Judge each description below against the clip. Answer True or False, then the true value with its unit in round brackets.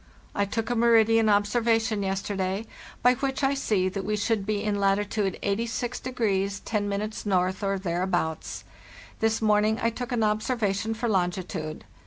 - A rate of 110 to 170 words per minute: True (150 wpm)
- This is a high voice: True (210 Hz)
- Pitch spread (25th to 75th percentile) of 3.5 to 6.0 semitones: False (2.6 semitones)